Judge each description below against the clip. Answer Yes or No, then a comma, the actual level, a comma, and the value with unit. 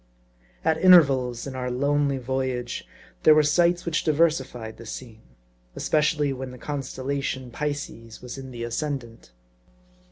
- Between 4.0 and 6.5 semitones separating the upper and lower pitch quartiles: No, average, 3.2 semitones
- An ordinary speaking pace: No, slow, 130 wpm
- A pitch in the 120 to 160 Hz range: Yes, low, 135 Hz